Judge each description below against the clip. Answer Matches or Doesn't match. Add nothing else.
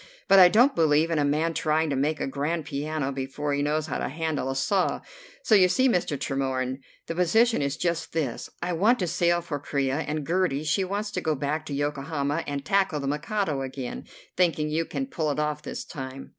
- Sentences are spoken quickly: Matches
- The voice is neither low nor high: Matches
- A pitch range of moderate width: Matches